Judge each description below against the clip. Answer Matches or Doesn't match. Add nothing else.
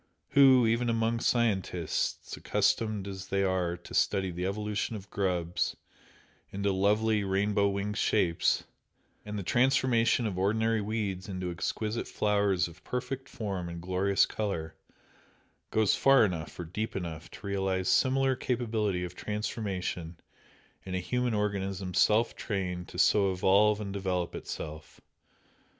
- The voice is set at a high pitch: Doesn't match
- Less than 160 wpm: Matches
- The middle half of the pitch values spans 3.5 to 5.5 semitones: Doesn't match